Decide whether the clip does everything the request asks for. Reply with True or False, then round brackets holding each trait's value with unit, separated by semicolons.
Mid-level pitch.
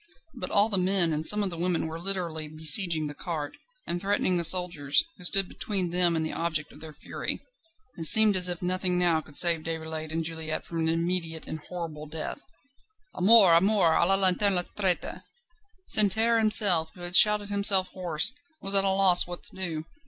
True (175 Hz)